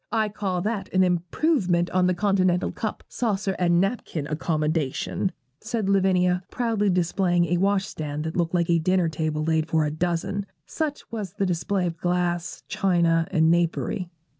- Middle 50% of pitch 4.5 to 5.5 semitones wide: No, average, 2.9 semitones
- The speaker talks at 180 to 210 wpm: No, average, 165 wpm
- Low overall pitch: No, medium, 180 Hz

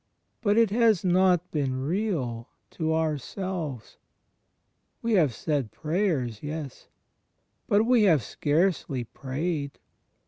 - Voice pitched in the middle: Yes, medium, 160 Hz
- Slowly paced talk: Yes, slow, 105 wpm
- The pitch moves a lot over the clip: Yes, wide, 5.7 semitones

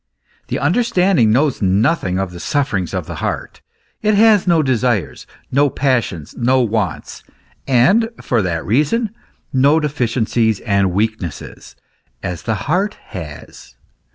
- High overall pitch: No, low, 120 Hz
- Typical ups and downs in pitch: No, wide, 7.4 semitones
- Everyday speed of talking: No, slow, 125 wpm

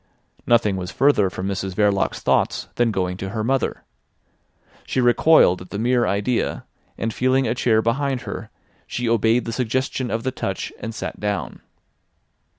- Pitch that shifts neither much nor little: Yes, average, 4.1 semitones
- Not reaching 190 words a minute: Yes, average, 160 wpm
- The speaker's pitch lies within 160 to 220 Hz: No, low, 115 Hz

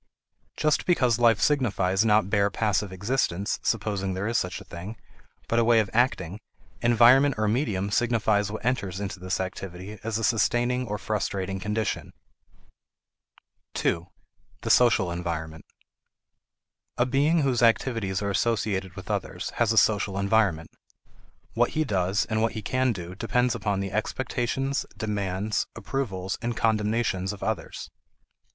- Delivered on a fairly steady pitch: No, average, 3.6 semitones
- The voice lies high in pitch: No, low, 105 Hz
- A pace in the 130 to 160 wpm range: Yes, average, 145 wpm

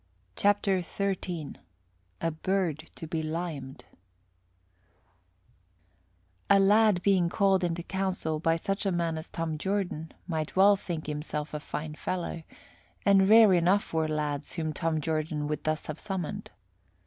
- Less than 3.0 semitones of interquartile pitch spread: No, average, 3.7 semitones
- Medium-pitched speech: Yes, medium, 170 Hz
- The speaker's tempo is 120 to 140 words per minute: Yes, slow, 135 wpm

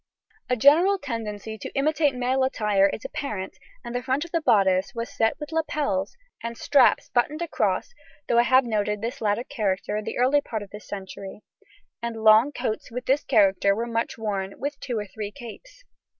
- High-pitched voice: Yes, high, 235 Hz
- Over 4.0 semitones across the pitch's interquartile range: Yes, average, 4.7 semitones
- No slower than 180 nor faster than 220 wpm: Yes, average, 190 wpm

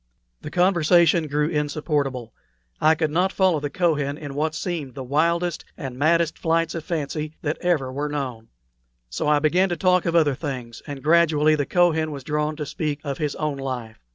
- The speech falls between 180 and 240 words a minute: Yes, average, 185 wpm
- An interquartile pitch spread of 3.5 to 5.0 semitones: No, average, 2.8 semitones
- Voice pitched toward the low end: No, medium, 150 Hz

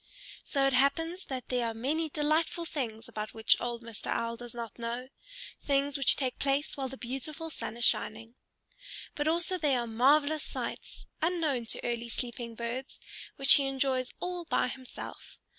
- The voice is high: Yes, very high, 265 Hz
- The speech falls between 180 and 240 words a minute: No, average, 170 wpm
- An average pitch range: Yes, average, 3.9 semitones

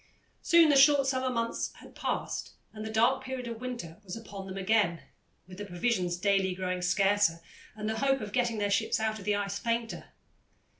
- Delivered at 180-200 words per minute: Yes, average, 195 wpm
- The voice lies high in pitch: Yes, high, 215 Hz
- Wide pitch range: No, average, 3.8 semitones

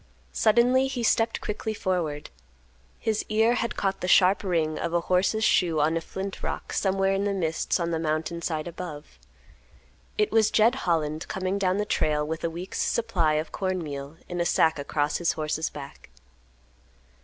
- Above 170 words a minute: Yes, average, 180 wpm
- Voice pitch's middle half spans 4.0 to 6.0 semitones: Yes, average, 4.4 semitones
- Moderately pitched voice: Yes, medium, 180 Hz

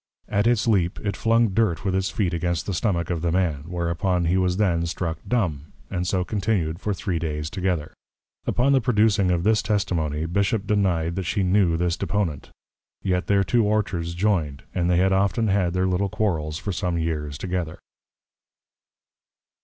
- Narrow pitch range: No, average, 3.2 semitones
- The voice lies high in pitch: No, very low, 90 Hz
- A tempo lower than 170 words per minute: No, average, 175 wpm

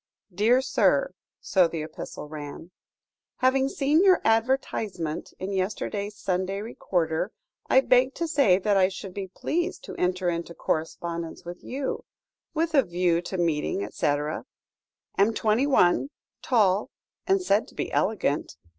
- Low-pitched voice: No, high, 195 Hz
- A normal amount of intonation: No, wide, 6.9 semitones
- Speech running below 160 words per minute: Yes, average, 140 wpm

